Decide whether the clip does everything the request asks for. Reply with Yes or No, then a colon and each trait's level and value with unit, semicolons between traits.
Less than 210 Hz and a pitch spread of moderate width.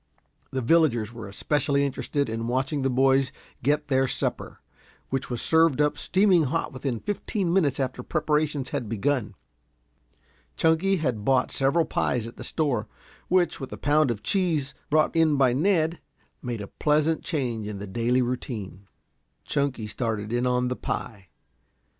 Yes: low, 135 Hz; average, 4.3 semitones